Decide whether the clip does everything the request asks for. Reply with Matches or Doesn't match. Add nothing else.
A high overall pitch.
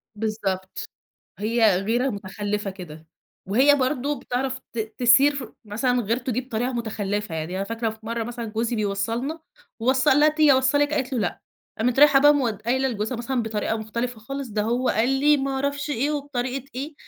Matches